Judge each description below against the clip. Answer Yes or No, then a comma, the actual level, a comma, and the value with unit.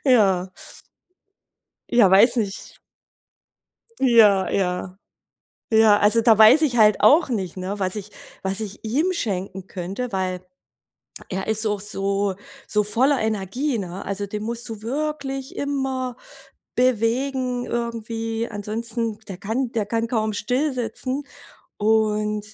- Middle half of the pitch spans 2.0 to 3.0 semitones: No, average, 3.7 semitones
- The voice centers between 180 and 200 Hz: No, high, 220 Hz